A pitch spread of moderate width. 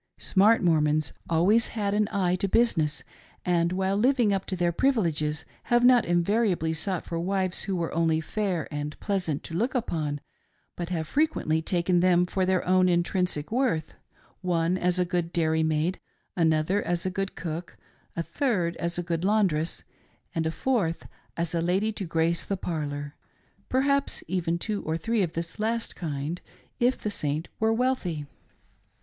Yes: average, 3.7 semitones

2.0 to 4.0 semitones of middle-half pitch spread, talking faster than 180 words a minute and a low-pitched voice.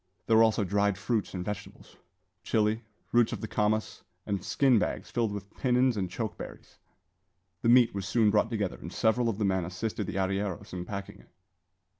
Yes: narrow, 2.6 semitones; average, 190 wpm; low, 105 Hz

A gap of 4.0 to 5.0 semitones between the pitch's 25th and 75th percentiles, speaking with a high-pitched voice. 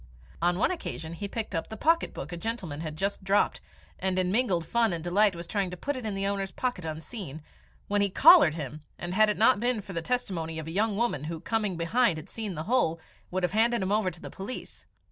Yes: average, 4.6 semitones; high, 195 Hz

